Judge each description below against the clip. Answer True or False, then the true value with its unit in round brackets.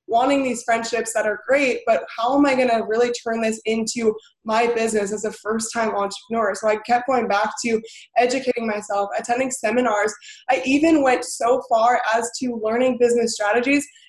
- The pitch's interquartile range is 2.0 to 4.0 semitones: True (2.4 semitones)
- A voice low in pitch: False (230 Hz)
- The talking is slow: False (180 wpm)